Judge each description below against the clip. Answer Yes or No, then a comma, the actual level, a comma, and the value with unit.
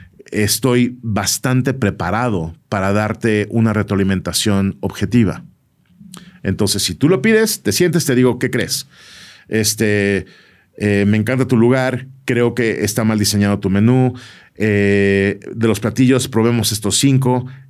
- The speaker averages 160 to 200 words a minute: No, average, 130 wpm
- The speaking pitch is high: No, low, 110 Hz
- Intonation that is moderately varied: Yes, average, 3.9 semitones